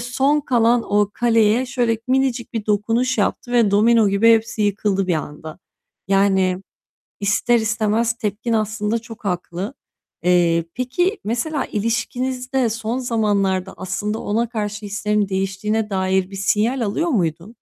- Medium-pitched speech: No, high, 215 Hz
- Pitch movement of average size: Yes, average, 3.1 semitones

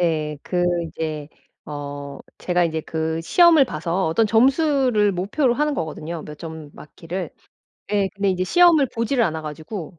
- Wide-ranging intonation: Yes, wide, 6.5 semitones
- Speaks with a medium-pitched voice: Yes, medium, 175 Hz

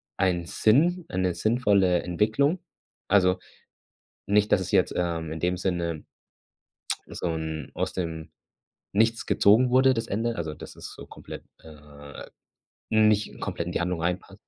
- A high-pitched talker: No, very low, 90 Hz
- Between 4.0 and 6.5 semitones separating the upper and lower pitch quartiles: Yes, average, 4.4 semitones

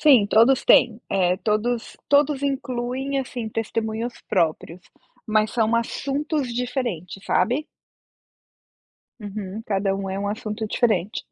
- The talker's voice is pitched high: Yes, high, 225 Hz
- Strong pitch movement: No, average, 3.8 semitones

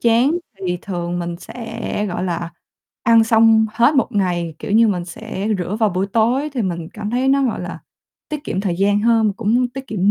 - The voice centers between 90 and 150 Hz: No, high, 215 Hz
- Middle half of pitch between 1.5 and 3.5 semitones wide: No, average, 4.3 semitones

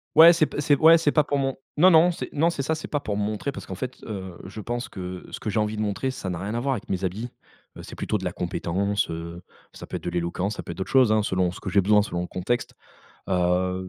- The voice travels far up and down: Yes, wide, 6.5 semitones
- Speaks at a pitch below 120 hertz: Yes, low, 105 Hz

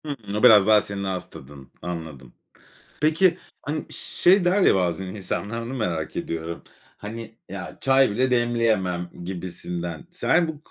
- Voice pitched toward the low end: Yes, low, 105 Hz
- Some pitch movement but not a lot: No, wide, 6.7 semitones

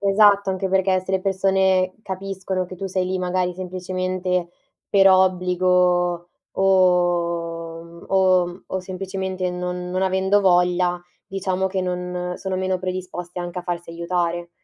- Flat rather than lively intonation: Yes, narrow, 1.1 semitones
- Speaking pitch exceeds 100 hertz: Yes, medium, 185 Hz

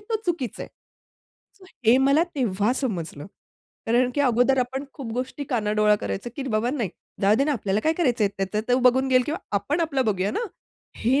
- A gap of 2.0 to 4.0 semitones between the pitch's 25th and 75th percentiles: No, average, 4.4 semitones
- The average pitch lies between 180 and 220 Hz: No, high, 245 Hz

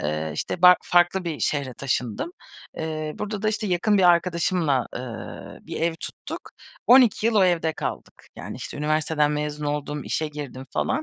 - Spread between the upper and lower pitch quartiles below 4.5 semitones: Yes, average, 3.7 semitones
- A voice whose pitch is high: No, medium, 160 Hz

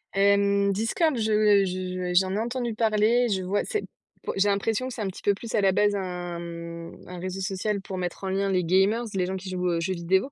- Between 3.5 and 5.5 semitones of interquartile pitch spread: No, narrow, 2.6 semitones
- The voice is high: Yes, high, 195 Hz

